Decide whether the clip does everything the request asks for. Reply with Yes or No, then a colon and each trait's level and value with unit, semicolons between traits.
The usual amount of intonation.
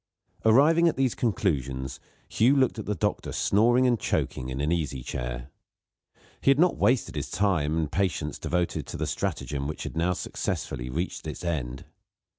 No: wide, 8.9 semitones